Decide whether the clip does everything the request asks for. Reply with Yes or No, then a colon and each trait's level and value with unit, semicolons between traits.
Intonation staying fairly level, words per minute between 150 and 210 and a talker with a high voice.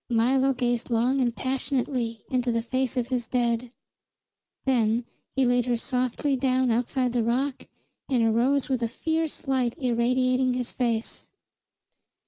No: narrow, 1.8 semitones; average, 140 wpm; very high, 250 Hz